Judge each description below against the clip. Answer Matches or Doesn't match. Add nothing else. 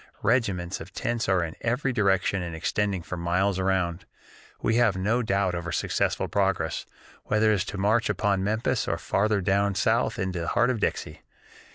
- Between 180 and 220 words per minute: Matches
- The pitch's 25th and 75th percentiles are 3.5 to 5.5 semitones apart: Doesn't match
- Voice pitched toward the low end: Matches